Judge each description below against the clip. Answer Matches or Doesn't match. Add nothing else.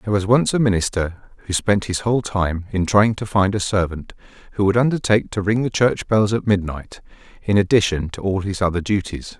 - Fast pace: Matches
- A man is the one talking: Matches